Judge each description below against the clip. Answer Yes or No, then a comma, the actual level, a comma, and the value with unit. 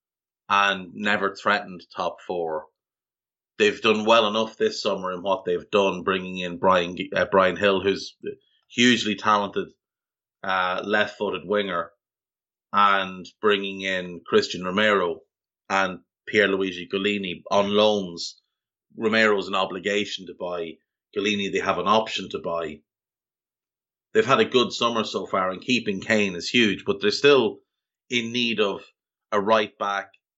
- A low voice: Yes, low, 100 Hz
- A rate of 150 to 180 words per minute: No, average, 140 wpm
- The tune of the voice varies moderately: No, narrow, 2.1 semitones